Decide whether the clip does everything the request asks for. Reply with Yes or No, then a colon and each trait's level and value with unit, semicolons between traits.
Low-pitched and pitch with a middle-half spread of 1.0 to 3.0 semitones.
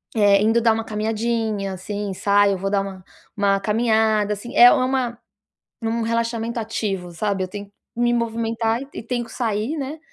No: high, 220 Hz; narrow, 2.5 semitones